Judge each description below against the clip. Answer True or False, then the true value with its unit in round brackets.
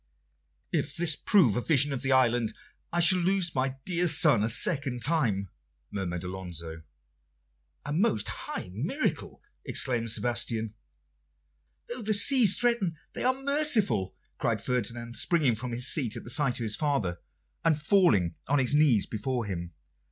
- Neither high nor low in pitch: False (130 Hz)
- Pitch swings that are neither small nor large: False (7.7 semitones)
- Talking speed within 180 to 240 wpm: False (150 wpm)